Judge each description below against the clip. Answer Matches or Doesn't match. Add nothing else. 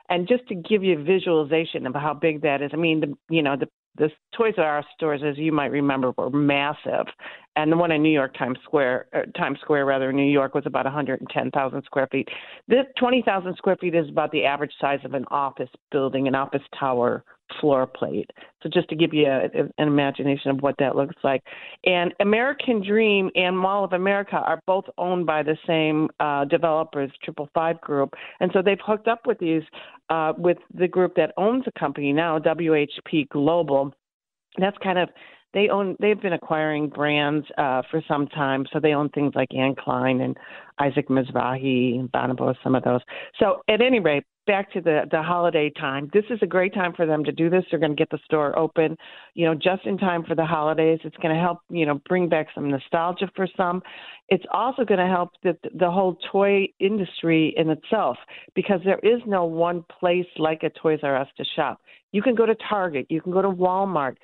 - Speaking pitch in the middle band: Matches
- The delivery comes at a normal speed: Doesn't match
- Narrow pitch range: Doesn't match